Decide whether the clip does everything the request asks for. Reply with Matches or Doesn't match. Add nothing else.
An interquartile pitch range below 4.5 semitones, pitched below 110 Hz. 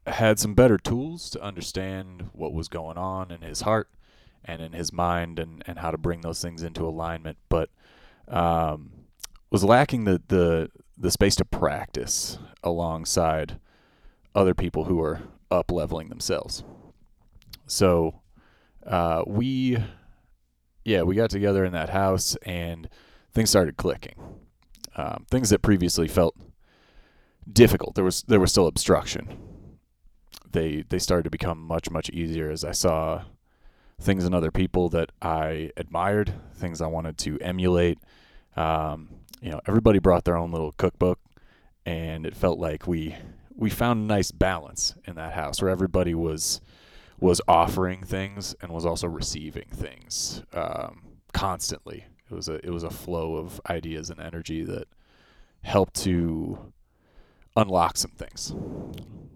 Matches